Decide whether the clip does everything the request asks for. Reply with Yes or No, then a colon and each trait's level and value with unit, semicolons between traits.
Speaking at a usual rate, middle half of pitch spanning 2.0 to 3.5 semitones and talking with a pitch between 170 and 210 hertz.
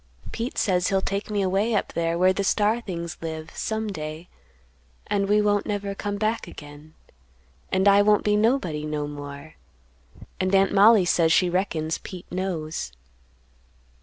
No: average, 160 wpm; average, 4.1 semitones; high, 190 Hz